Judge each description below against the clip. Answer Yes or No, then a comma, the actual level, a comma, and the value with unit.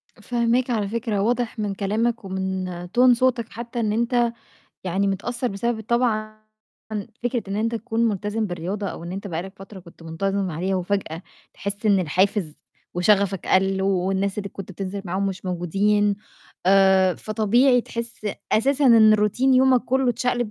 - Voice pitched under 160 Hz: No, high, 205 Hz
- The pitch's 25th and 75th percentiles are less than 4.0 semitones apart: Yes, average, 3.5 semitones